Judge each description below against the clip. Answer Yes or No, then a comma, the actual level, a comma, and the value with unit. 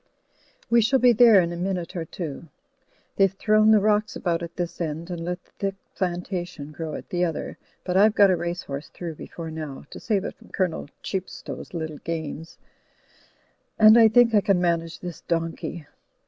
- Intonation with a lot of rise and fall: No, average, 3.5 semitones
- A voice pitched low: No, medium, 175 Hz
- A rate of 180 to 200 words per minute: Yes, average, 190 wpm